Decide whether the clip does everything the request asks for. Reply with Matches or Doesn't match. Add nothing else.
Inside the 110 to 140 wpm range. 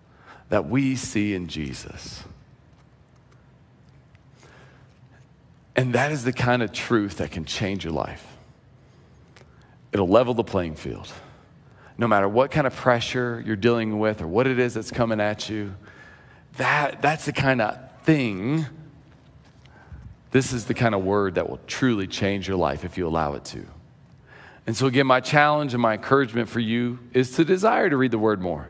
Doesn't match